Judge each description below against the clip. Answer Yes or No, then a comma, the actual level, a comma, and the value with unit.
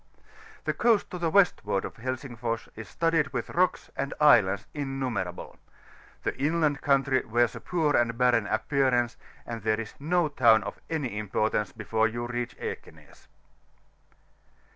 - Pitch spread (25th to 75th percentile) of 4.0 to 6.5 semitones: Yes, average, 4.7 semitones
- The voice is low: Yes, low, 125 Hz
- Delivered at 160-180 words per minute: No, average, 145 wpm